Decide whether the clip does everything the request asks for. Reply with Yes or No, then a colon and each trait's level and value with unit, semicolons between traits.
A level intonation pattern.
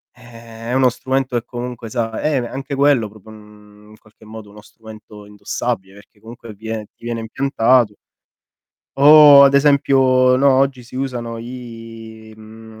No: average, 3.0 semitones